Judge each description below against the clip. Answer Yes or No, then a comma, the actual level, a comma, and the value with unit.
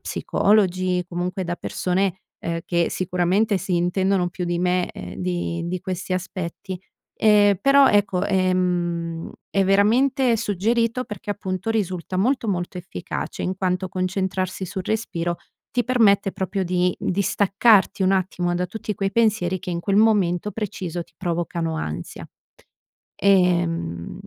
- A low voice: No, medium, 185 Hz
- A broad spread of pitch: No, narrow, 2.4 semitones